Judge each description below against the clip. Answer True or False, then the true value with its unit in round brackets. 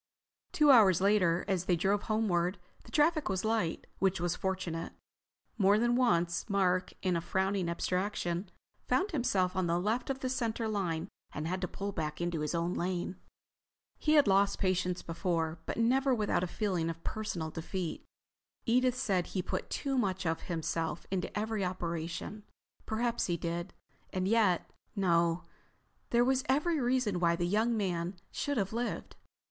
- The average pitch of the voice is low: False (190 Hz)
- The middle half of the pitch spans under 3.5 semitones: False (4.4 semitones)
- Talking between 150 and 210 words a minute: True (165 wpm)